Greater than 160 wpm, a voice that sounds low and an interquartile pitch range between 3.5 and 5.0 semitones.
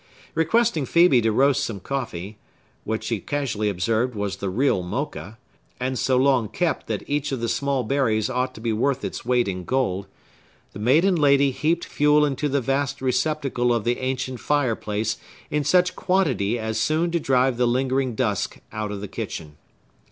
Yes: average, 170 wpm; low, 130 Hz; average, 4.3 semitones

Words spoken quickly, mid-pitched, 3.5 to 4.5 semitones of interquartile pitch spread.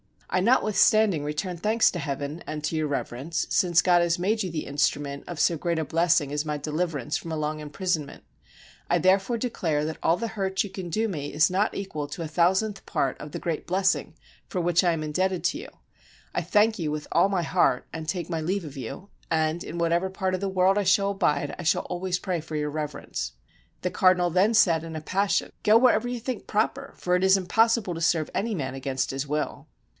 Yes: fast, 225 wpm; medium, 175 Hz; average, 4.0 semitones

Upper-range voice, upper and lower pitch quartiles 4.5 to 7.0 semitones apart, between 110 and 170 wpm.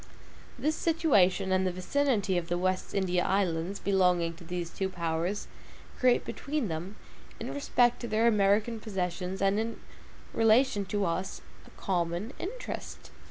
No: high, 195 Hz; average, 4.1 semitones; average, 145 wpm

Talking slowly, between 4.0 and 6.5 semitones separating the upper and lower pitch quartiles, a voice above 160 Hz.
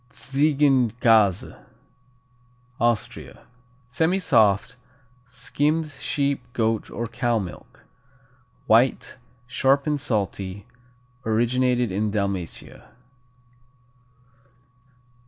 No: slow, 65 wpm; average, 4.3 semitones; low, 120 Hz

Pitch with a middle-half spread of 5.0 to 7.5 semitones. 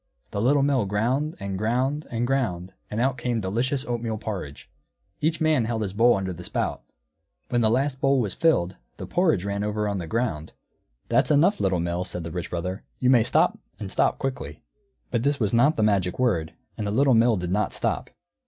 Yes: wide, 5.5 semitones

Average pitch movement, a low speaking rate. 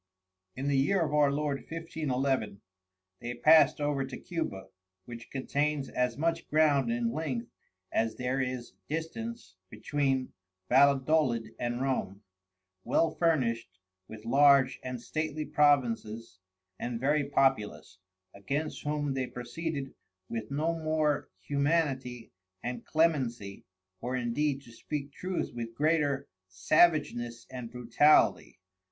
Yes: average, 3.9 semitones; slow, 120 wpm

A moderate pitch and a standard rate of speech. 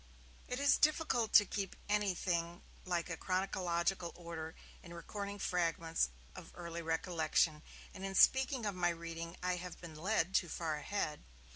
Yes: medium, 175 Hz; average, 145 wpm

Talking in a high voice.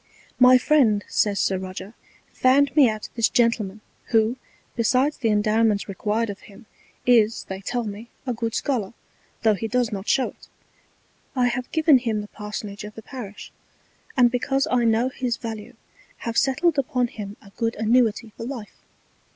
Yes: high, 230 Hz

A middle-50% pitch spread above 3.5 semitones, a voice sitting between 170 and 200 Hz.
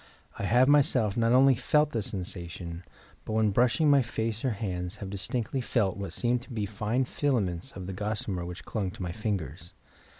No: average, 4.6 semitones; low, 105 Hz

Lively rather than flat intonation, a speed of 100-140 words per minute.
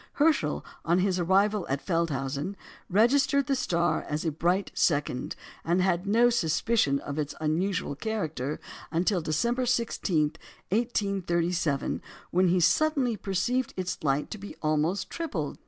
Yes: wide, 5.8 semitones; slow, 135 wpm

